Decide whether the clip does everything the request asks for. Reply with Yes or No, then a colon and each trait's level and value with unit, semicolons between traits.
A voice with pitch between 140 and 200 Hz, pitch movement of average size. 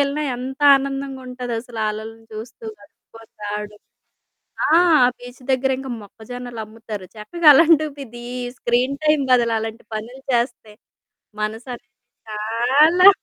No: high, 240 Hz; average, 3.4 semitones